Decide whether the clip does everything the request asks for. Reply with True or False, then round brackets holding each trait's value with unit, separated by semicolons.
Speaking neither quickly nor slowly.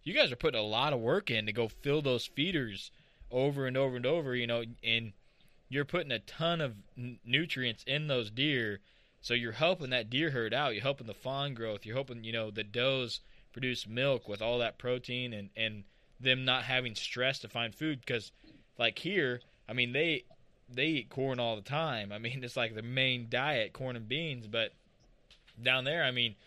False (210 wpm)